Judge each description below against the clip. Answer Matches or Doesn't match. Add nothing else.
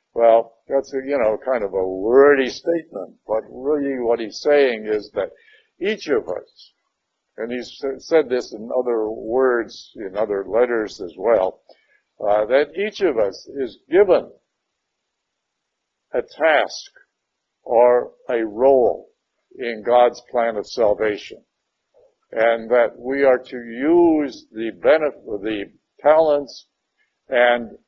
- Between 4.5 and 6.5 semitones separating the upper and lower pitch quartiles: Matches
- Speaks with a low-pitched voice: Matches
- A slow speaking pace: Matches